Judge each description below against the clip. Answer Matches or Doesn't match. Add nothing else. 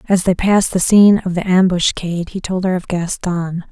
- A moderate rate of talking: Doesn't match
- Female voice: Matches